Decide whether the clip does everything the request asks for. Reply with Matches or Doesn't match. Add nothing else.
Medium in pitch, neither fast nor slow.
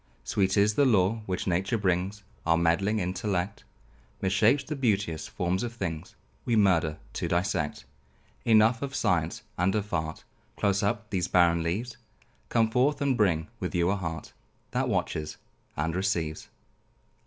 Doesn't match